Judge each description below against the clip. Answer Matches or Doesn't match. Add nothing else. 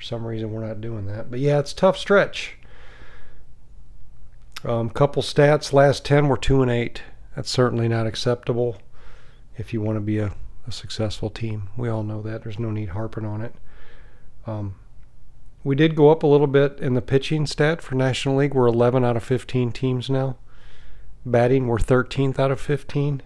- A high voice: Doesn't match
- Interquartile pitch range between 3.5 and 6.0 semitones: Doesn't match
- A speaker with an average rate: Matches